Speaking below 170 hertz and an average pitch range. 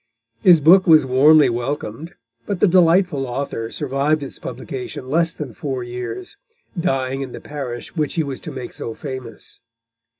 Yes: medium, 140 Hz; average, 4.1 semitones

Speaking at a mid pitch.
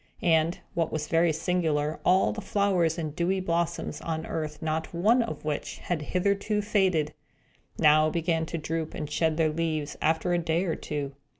Yes: medium, 165 Hz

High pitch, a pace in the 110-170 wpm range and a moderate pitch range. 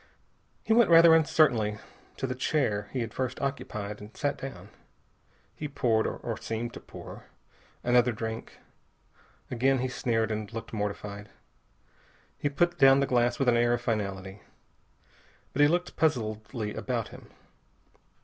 No: low, 120 Hz; average, 145 wpm; average, 4.1 semitones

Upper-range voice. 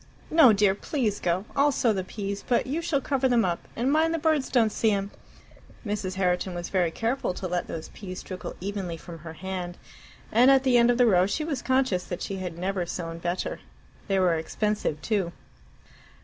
Yes: high, 200 Hz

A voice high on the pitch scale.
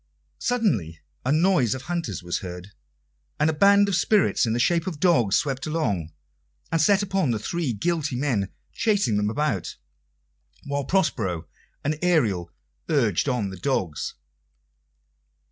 No: medium, 140 Hz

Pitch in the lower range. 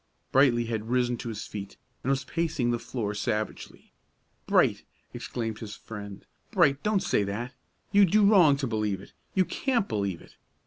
Yes: low, 120 Hz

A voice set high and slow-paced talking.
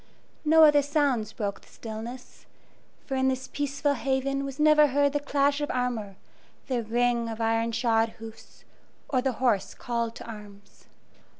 No: very high, 250 Hz; average, 160 wpm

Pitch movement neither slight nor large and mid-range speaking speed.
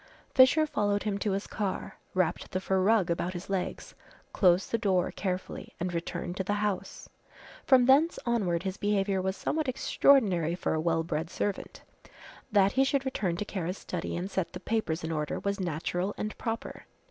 Yes: average, 3.2 semitones; average, 180 wpm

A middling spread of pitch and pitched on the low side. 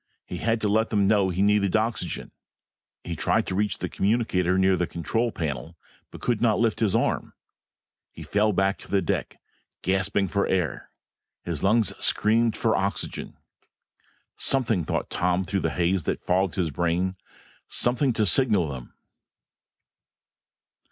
Yes: average, 3.5 semitones; low, 100 Hz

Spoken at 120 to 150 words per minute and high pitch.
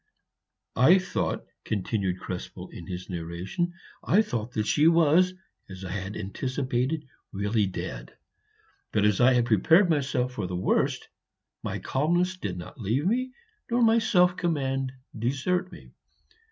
No: average, 140 wpm; low, 130 Hz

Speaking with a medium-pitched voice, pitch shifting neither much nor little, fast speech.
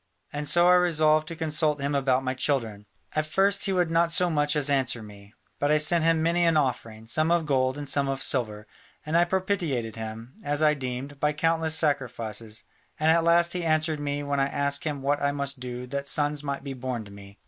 Yes: medium, 145 Hz; average, 3.7 semitones; fast, 225 wpm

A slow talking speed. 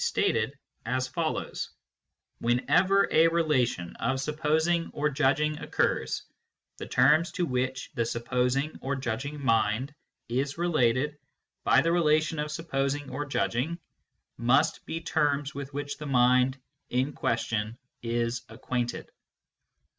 Yes: slow, 115 wpm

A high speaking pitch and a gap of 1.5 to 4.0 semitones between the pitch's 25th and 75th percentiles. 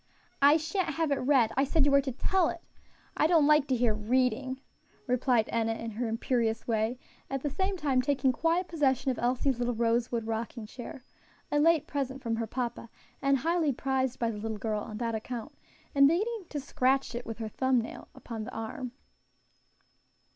Yes: very high, 255 Hz; average, 3.7 semitones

